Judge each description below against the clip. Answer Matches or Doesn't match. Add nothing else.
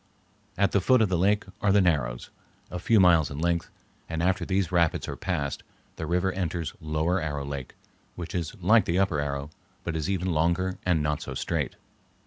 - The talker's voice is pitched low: Matches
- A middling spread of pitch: Matches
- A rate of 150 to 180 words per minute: Doesn't match